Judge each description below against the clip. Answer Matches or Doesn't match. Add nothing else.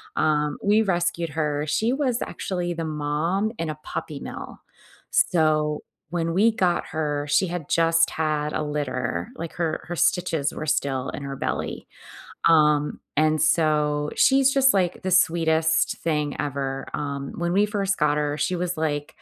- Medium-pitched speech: Matches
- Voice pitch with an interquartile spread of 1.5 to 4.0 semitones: Matches